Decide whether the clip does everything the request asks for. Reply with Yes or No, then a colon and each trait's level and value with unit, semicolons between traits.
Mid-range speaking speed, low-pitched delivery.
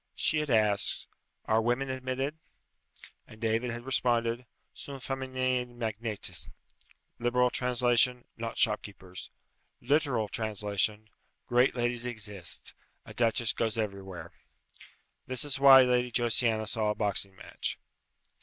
No: slow, 115 wpm; low, 120 Hz